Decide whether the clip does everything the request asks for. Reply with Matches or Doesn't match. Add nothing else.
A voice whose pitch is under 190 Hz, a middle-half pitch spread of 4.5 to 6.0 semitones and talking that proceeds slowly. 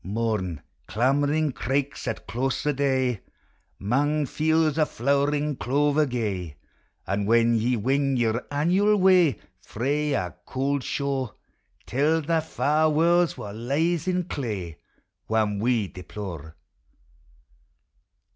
Matches